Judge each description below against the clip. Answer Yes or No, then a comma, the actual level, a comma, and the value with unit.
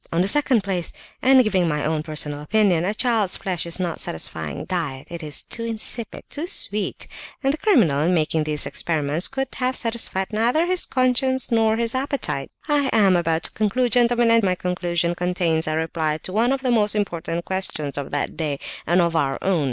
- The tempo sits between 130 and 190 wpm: No, average, 200 wpm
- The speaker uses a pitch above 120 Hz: Yes, high, 190 Hz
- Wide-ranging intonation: Yes, wide, 6.5 semitones